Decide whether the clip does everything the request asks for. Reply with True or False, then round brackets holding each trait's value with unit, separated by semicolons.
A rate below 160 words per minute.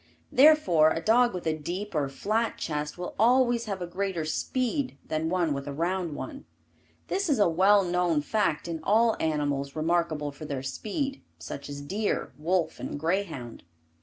False (170 wpm)